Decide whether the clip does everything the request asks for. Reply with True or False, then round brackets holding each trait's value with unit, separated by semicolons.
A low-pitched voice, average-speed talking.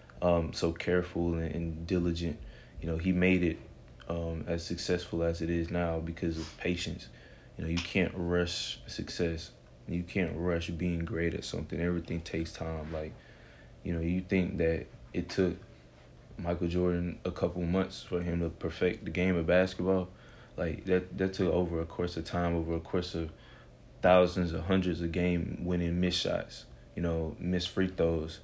True (85 Hz; 175 wpm)